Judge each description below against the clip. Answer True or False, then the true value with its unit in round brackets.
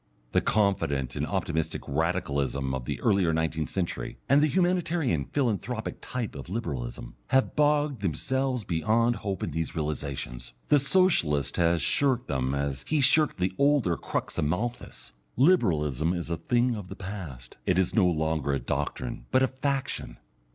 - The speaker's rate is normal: True (160 wpm)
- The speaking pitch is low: True (90 Hz)